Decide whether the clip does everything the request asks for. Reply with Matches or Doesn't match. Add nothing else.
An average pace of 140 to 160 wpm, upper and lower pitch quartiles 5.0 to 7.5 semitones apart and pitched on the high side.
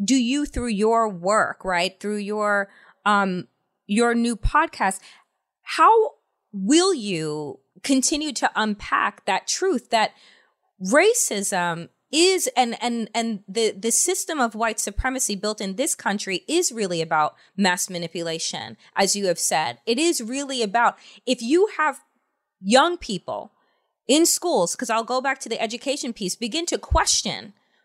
Matches